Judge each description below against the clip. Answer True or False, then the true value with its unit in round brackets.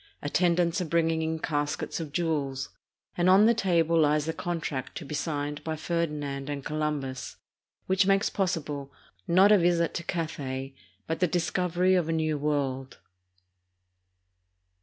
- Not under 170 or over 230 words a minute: False (150 wpm)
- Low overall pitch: False (160 Hz)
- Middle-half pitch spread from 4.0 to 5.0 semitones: False (3.0 semitones)